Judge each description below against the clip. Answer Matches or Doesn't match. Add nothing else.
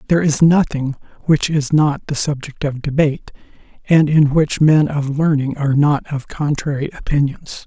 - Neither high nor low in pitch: Matches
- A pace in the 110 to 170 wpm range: Matches